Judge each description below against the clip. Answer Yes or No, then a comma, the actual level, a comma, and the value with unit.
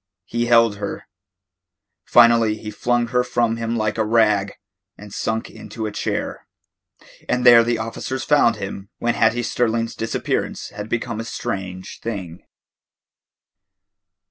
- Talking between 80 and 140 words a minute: Yes, slow, 135 wpm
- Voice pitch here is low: Yes, low, 115 Hz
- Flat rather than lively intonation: Yes, narrow, 1.8 semitones